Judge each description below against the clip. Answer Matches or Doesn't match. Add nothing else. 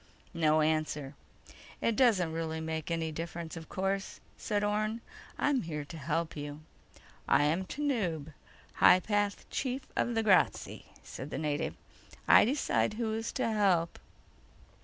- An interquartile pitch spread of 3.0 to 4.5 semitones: Doesn't match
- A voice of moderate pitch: Matches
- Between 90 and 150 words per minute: Matches